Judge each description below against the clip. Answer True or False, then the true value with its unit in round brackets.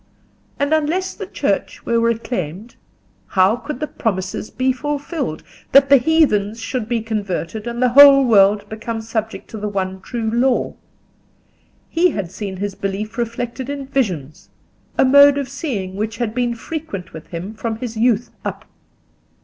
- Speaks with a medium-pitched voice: False (230 Hz)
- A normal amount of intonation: True (4.8 semitones)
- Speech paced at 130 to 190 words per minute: True (155 wpm)